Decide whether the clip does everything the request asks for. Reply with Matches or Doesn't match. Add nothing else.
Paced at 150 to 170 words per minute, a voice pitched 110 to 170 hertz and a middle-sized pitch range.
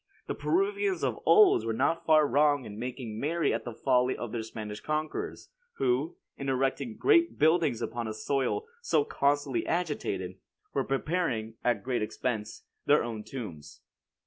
Doesn't match